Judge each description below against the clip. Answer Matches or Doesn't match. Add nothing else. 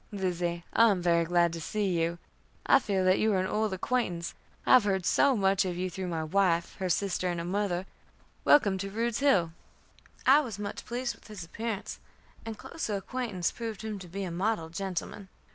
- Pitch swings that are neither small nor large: Matches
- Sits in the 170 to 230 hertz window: Matches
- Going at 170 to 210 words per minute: Matches